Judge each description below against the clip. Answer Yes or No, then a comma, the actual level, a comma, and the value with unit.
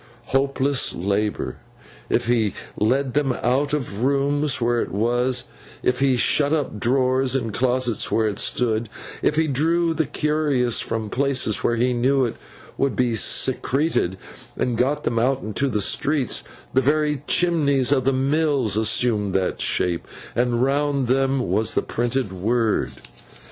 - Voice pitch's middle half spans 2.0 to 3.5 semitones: Yes, average, 3.2 semitones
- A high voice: No, low, 130 Hz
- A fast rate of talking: No, average, 150 wpm